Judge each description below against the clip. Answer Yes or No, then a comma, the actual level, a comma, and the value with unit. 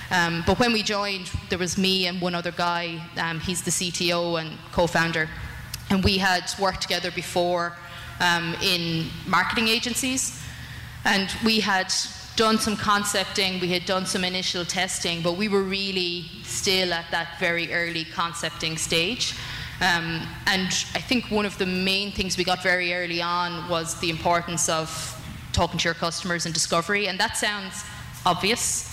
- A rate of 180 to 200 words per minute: No, average, 165 wpm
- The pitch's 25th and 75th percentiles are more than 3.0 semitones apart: No, narrow, 2.4 semitones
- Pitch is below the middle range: No, medium, 180 Hz